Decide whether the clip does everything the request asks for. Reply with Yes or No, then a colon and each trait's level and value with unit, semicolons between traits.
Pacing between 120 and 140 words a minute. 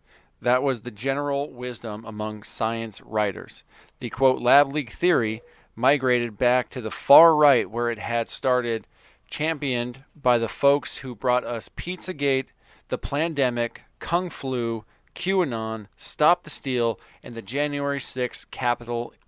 Yes: slow, 135 wpm